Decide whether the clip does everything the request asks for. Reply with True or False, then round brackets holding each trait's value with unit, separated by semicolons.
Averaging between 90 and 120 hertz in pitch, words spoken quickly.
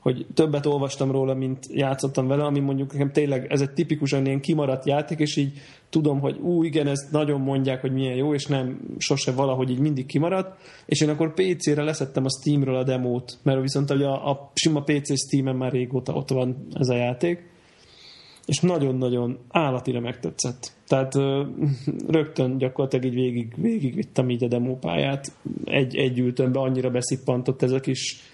False (135 Hz; 170 wpm)